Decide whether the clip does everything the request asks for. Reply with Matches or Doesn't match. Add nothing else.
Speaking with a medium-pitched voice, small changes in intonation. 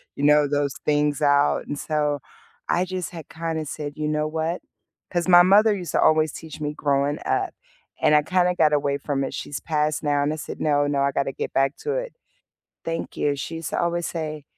Matches